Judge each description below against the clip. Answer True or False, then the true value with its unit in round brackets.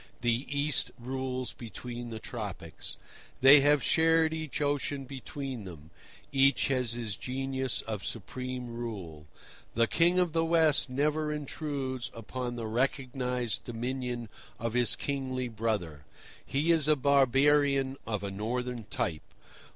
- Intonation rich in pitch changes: False (3.5 semitones)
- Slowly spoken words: True (130 wpm)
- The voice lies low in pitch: True (130 Hz)